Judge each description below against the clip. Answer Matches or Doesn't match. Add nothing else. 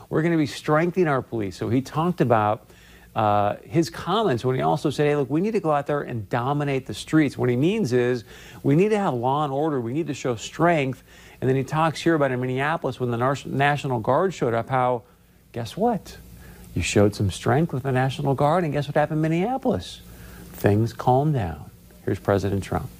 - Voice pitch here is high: Doesn't match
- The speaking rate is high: Matches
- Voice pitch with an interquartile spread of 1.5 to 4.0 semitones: Doesn't match